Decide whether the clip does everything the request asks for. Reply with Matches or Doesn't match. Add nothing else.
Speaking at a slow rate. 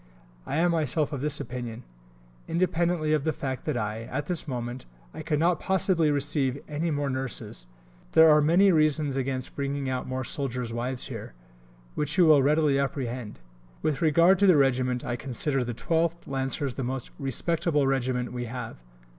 Doesn't match